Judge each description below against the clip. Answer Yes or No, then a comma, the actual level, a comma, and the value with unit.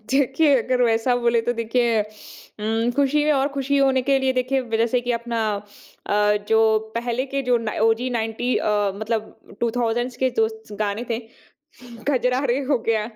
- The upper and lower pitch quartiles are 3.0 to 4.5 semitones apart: No, narrow, 2.6 semitones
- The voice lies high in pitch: Yes, high, 240 Hz